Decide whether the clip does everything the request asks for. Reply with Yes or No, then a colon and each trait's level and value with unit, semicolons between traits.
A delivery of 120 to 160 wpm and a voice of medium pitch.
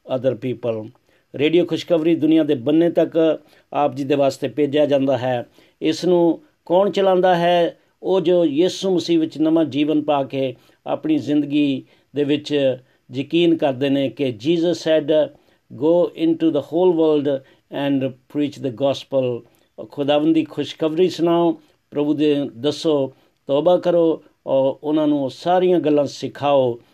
Yes: average, 135 wpm; medium, 150 Hz